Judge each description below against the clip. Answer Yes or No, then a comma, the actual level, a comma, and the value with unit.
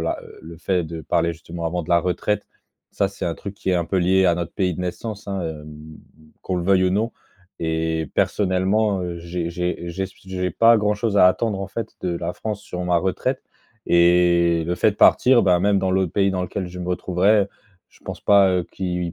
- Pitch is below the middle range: Yes, very low, 90 Hz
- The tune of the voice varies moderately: No, narrow, 2.3 semitones